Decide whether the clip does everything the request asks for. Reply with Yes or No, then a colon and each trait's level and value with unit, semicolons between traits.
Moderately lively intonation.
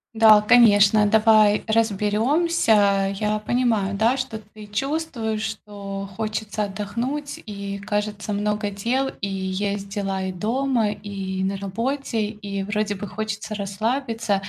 No: narrow, 2.0 semitones